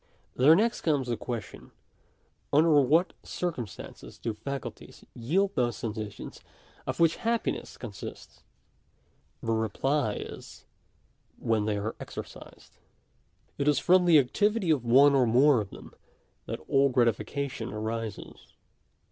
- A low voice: Yes, low, 130 Hz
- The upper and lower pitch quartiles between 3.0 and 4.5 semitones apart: No, wide, 5.5 semitones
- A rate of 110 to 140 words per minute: Yes, slow, 135 wpm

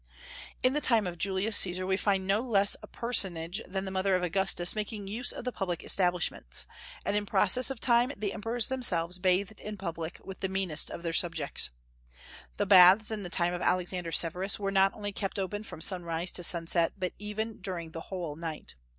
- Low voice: No, high, 190 Hz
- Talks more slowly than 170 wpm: No, average, 200 wpm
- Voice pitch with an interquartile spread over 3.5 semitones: No, average, 3.0 semitones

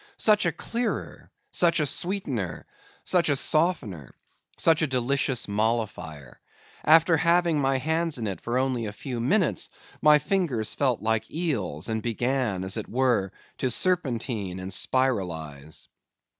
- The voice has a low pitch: Yes, low, 130 Hz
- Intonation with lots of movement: Yes, wide, 7.4 semitones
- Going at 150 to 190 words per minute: No, average, 140 wpm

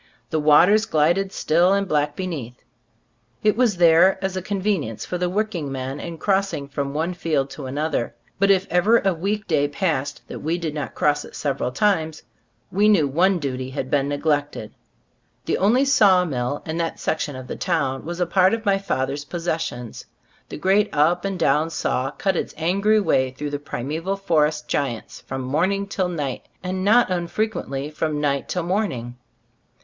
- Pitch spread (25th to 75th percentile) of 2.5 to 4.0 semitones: No, average, 5.0 semitones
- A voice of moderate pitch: Yes, medium, 165 Hz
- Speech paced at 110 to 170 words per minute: No, average, 180 wpm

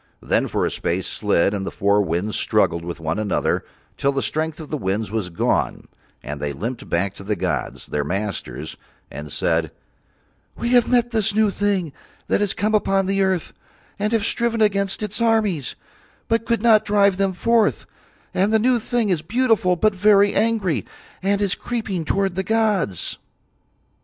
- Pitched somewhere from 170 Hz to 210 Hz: Yes, high, 190 Hz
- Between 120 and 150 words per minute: No, average, 175 wpm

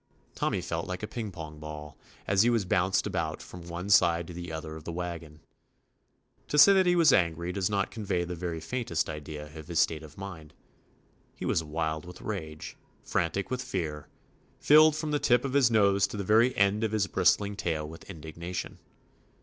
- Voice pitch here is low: Yes, very low, 90 Hz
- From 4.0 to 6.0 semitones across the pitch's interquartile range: Yes, average, 4.8 semitones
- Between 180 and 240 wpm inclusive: Yes, fast, 205 wpm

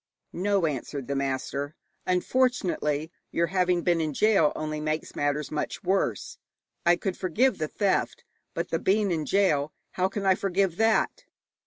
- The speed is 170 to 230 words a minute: No, average, 155 wpm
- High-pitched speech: No, medium, 175 Hz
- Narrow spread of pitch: No, average, 4.4 semitones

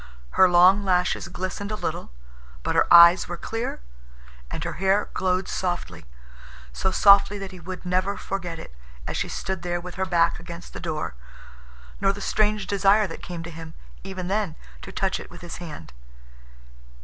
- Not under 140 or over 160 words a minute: No, average, 170 wpm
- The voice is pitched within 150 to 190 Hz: Yes, medium, 185 Hz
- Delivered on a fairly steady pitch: Yes, narrow, 2.3 semitones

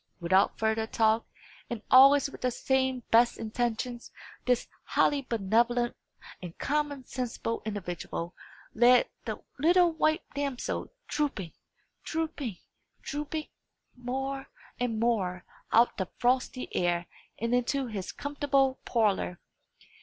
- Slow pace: Yes, slow, 115 wpm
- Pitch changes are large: No, average, 3.8 semitones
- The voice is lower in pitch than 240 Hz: No, high, 245 Hz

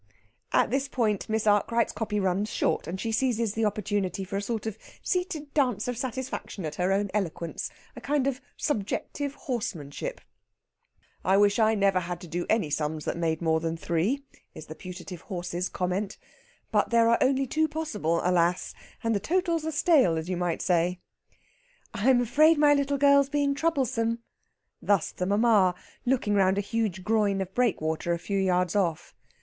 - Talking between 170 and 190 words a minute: Yes, average, 175 wpm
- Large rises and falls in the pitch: Yes, wide, 5.9 semitones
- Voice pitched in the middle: No, high, 205 Hz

